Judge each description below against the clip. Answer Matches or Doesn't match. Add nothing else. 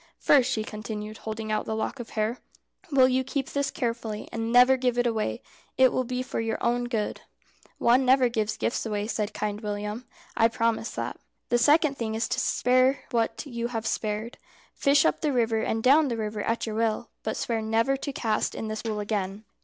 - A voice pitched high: Matches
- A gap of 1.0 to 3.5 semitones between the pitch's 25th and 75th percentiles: Matches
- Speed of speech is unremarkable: Doesn't match